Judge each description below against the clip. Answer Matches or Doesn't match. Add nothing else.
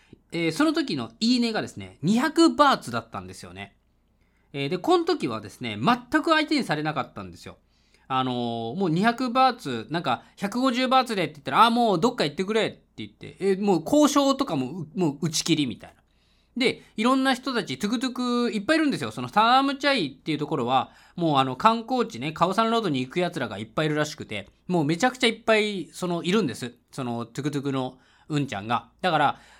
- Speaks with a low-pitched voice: Doesn't match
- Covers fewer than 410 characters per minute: Doesn't match